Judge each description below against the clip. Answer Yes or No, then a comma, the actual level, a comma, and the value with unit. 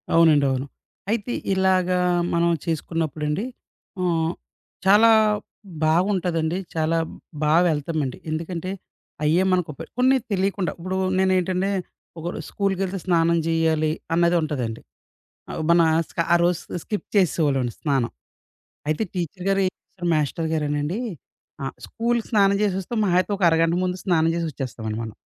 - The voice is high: No, medium, 170 Hz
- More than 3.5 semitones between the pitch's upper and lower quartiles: No, average, 3.2 semitones